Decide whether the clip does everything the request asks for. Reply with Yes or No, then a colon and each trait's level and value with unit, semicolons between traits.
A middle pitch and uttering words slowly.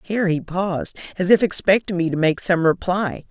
No: medium, 180 Hz; average, 200 wpm